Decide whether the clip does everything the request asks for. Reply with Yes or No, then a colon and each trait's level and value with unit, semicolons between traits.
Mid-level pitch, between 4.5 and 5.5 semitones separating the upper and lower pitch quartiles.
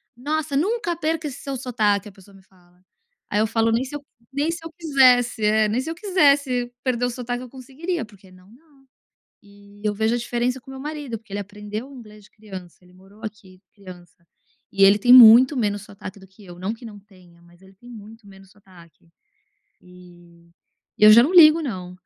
No: high, 220 Hz; average, 5.1 semitones